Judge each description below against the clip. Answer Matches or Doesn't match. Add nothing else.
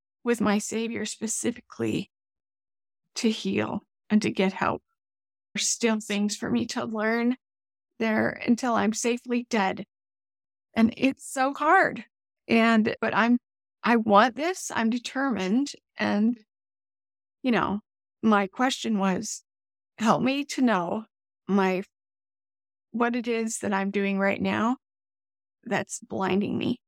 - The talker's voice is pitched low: Doesn't match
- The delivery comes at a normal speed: Doesn't match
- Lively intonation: Doesn't match